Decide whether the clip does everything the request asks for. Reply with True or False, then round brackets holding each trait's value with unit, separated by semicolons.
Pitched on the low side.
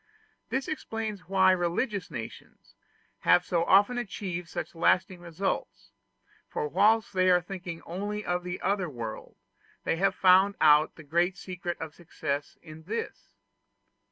False (180 Hz)